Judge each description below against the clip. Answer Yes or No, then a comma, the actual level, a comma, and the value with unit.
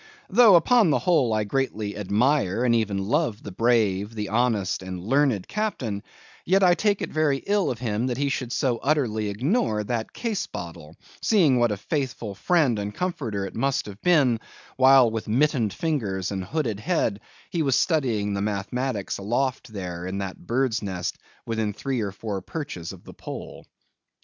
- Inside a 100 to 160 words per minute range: No, average, 175 wpm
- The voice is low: Yes, low, 115 Hz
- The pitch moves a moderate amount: No, wide, 5.8 semitones